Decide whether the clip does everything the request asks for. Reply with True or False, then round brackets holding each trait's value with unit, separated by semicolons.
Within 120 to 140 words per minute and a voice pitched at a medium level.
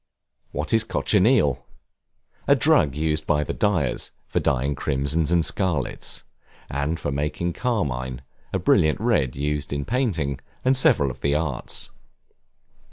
False (135 wpm; 75 Hz)